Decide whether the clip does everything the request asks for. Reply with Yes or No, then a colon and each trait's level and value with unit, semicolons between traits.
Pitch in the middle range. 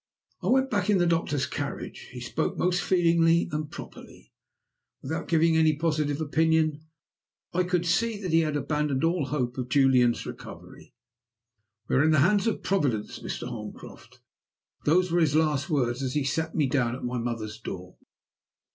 Yes: medium, 155 Hz